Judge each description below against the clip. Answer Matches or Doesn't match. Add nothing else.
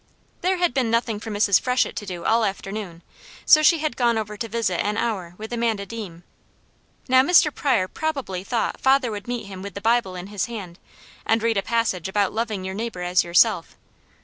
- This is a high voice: Matches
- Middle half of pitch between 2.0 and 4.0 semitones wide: Matches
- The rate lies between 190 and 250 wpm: Matches